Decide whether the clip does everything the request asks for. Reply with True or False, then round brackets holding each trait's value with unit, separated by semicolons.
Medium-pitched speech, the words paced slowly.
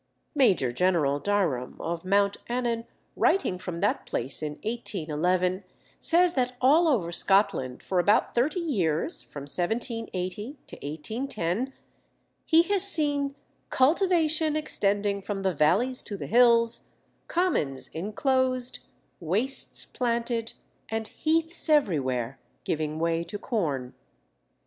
False (205 Hz; 110 wpm)